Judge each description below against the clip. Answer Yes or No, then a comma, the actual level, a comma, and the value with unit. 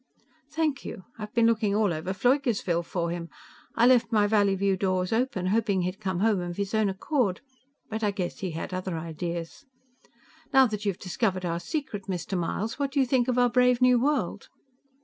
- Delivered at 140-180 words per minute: No, average, 190 wpm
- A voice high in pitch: Yes, high, 205 Hz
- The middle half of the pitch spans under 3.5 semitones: No, average, 4.7 semitones